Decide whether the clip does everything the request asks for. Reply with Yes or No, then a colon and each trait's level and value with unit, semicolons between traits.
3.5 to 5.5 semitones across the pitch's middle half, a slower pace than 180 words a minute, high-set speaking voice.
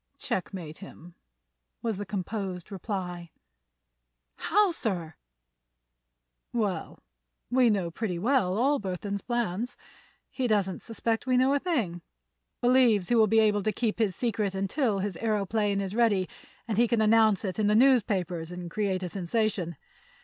Yes: average, 3.8 semitones; average, 145 wpm; high, 210 Hz